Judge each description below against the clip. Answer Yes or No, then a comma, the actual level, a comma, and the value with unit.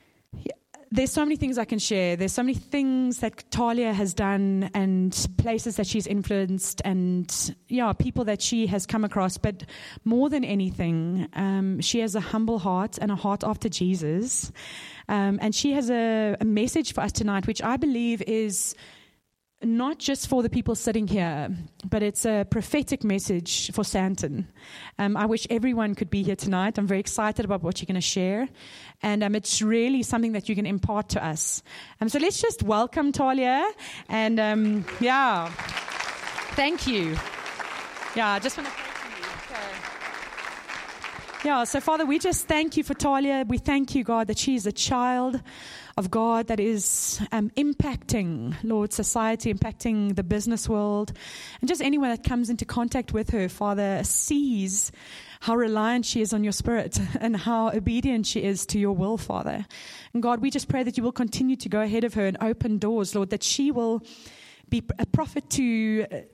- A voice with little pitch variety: No, average, 3.6 semitones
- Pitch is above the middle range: Yes, high, 220 Hz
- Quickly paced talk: No, average, 180 wpm